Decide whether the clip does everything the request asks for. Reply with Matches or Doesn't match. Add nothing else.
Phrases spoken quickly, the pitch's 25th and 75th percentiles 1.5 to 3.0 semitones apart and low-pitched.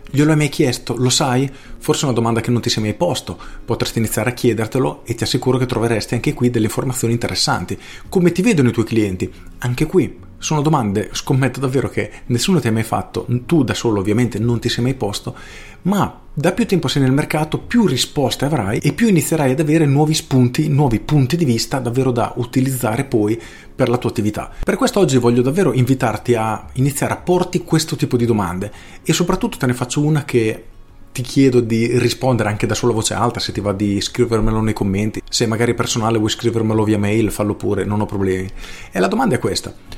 Doesn't match